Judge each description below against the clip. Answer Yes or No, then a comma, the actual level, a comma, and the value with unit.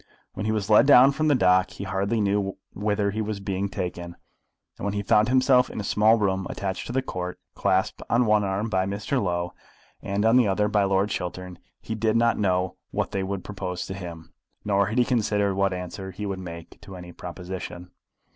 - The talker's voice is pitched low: Yes, low, 100 Hz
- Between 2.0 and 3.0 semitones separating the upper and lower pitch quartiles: Yes, narrow, 2.5 semitones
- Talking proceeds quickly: Yes, fast, 215 wpm